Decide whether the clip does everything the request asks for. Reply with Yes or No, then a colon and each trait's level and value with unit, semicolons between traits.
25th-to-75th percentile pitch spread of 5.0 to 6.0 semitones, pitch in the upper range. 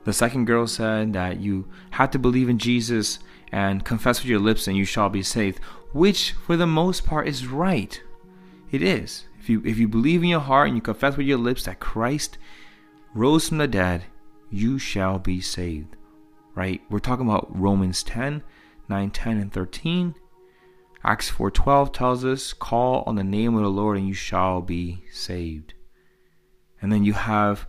No: wide, 5.5 semitones; low, 110 Hz